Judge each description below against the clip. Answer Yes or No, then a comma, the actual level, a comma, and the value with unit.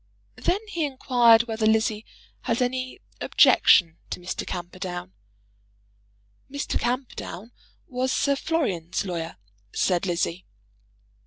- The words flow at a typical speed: No, slow, 100 wpm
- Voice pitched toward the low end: No, high, 225 Hz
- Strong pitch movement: Yes, wide, 6.3 semitones